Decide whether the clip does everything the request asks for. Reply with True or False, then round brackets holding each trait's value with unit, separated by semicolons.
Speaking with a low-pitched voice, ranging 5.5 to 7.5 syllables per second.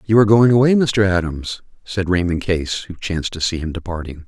True (95 Hz; 5.6 syllables/s)